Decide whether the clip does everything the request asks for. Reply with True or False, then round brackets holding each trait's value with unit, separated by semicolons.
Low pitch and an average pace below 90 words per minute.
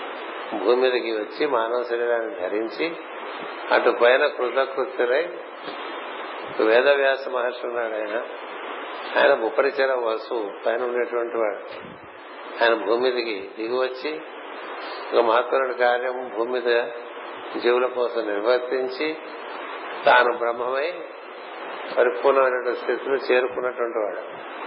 True (125 Hz; 80 wpm)